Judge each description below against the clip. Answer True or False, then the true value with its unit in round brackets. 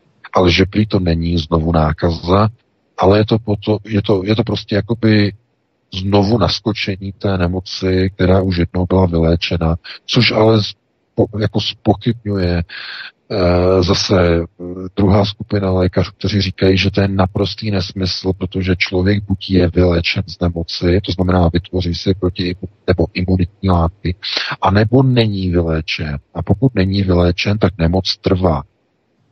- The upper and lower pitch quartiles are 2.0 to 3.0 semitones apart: True (2.4 semitones)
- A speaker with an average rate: True (140 wpm)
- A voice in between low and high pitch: False (95 Hz)